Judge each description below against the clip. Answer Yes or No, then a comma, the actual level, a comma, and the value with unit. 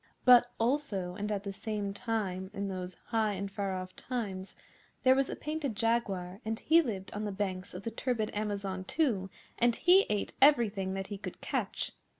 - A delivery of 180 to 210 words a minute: Yes, average, 185 wpm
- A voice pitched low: No, high, 205 Hz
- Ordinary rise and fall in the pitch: Yes, average, 3.7 semitones